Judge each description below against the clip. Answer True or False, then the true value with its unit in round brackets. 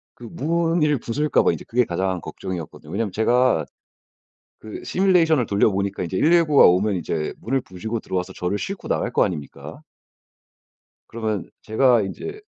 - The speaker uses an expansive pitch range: True (7.3 semitones)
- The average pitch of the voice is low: True (110 Hz)